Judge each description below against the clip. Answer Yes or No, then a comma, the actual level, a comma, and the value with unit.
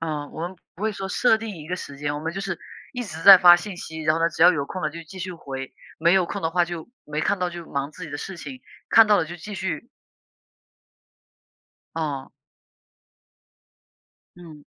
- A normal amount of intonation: Yes, average, 3.4 semitones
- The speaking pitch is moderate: Yes, medium, 170 Hz